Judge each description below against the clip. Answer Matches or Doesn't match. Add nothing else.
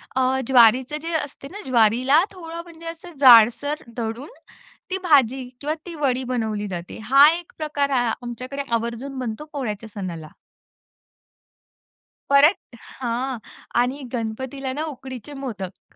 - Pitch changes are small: Doesn't match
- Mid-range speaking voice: Doesn't match